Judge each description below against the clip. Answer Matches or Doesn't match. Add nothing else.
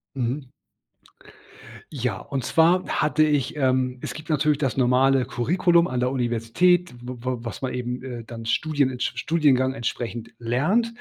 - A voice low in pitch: Matches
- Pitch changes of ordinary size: Matches